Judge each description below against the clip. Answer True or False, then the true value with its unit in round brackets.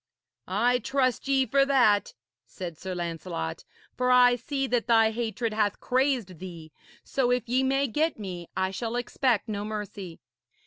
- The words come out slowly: False (160 wpm)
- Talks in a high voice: True (230 Hz)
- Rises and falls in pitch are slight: False (5.0 semitones)